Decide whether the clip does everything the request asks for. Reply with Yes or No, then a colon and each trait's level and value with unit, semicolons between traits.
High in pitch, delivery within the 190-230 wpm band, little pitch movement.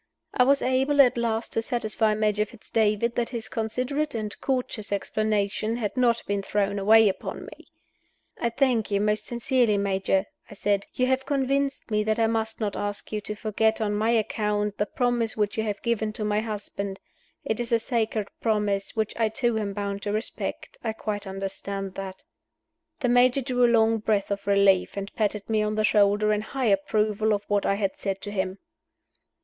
Yes: high, 215 Hz; average, 195 wpm; narrow, 2.3 semitones